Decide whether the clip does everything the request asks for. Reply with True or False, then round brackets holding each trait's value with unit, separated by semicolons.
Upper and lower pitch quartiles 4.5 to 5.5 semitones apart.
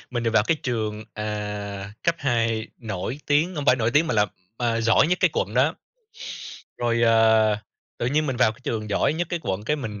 True (4.8 semitones)